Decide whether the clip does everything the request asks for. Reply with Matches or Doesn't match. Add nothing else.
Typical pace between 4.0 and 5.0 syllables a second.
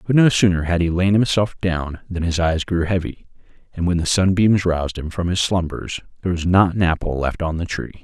Doesn't match